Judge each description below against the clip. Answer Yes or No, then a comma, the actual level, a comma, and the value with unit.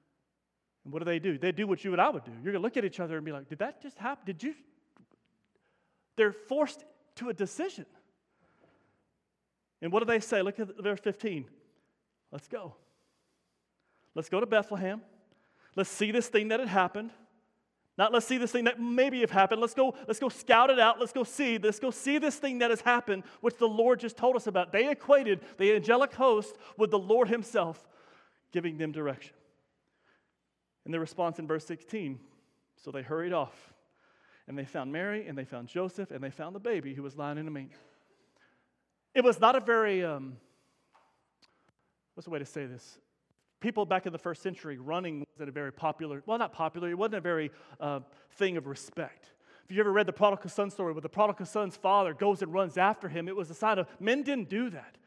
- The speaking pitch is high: Yes, high, 200 Hz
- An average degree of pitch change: No, wide, 6.0 semitones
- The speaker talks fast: Yes, fast, 210 wpm